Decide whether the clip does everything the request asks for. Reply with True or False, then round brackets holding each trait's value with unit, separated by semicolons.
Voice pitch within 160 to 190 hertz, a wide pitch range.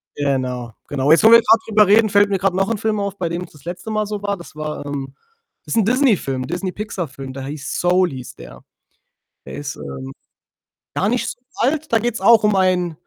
True (185 Hz; 6.9 semitones)